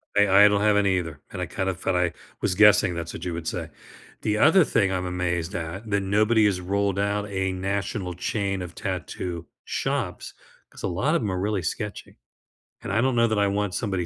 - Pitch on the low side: Yes, low, 100 Hz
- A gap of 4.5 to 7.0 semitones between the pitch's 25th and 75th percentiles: No, narrow, 2.5 semitones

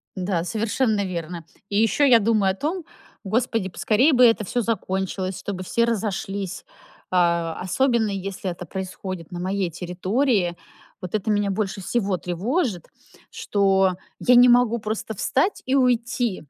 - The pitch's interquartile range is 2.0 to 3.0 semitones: No, average, 4.1 semitones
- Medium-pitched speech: No, high, 200 Hz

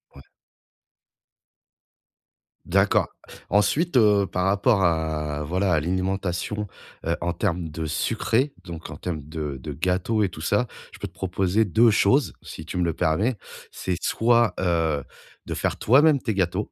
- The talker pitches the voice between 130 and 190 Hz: No, very low, 95 Hz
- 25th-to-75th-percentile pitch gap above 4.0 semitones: Yes, average, 4.6 semitones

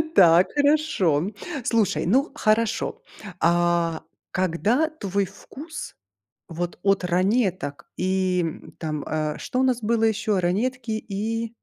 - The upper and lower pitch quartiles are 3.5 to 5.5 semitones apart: Yes, average, 4.9 semitones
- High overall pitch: Yes, high, 195 Hz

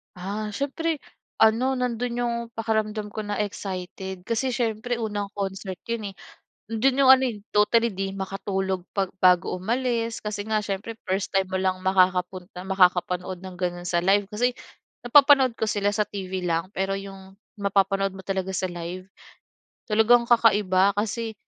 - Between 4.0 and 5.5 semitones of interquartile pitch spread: No, average, 3.1 semitones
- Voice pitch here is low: No, high, 200 Hz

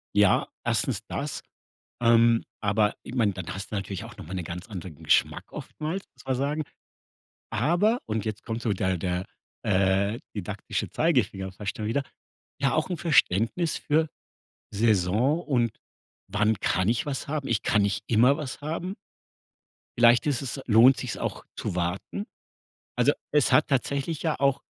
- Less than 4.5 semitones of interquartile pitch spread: No, wide, 6.1 semitones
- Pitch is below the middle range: Yes, low, 115 Hz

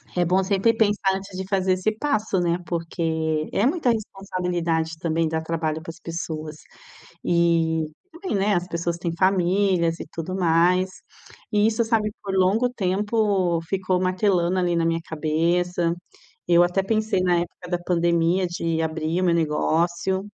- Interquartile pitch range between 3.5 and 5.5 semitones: No, narrow, 2.6 semitones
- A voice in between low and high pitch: Yes, medium, 180 Hz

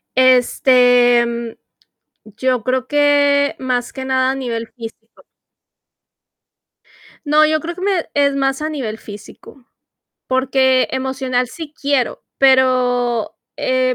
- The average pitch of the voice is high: Yes, very high, 260 Hz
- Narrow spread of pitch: Yes, narrow, 2.2 semitones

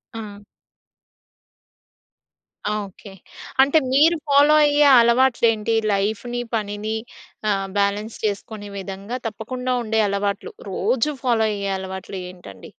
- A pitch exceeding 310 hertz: No, high, 220 Hz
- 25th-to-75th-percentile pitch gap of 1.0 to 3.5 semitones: No, average, 3.9 semitones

